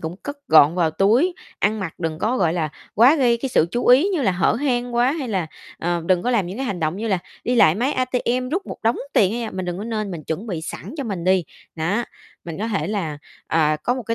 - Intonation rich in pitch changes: Yes, wide, 6.0 semitones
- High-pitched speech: Yes, high, 210 Hz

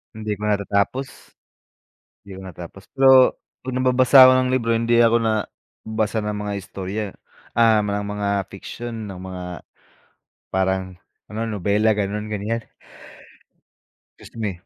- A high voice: No, low, 105 Hz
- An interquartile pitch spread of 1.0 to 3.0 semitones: Yes, narrow, 2.6 semitones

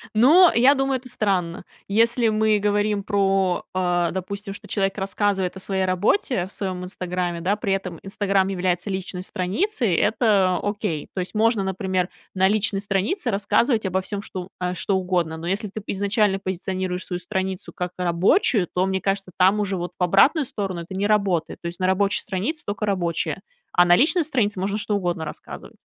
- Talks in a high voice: Yes, high, 195 Hz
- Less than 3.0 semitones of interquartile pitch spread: Yes, narrow, 2.5 semitones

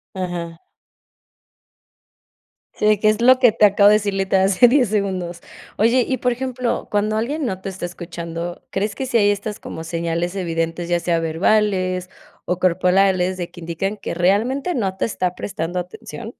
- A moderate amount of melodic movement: Yes, average, 3.6 semitones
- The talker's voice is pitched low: No, high, 190 Hz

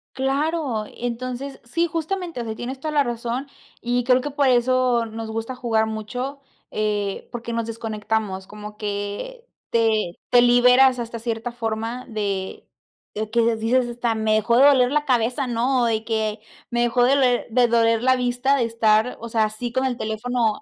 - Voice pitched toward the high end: Yes, high, 235 Hz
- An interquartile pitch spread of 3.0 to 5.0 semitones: No, narrow, 2.5 semitones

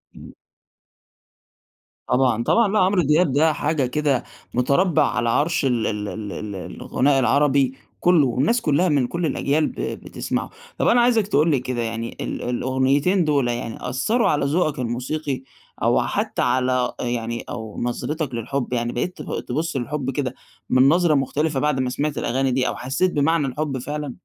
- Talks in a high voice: No, low, 135 Hz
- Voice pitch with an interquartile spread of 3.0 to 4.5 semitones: Yes, average, 3.7 semitones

